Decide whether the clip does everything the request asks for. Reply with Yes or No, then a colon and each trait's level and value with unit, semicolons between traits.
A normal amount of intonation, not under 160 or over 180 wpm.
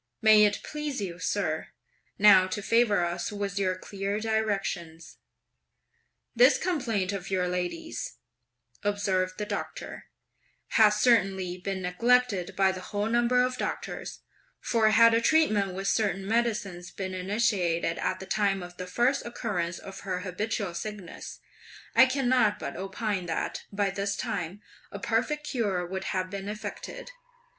No: average, 3.6 semitones; average, 145 wpm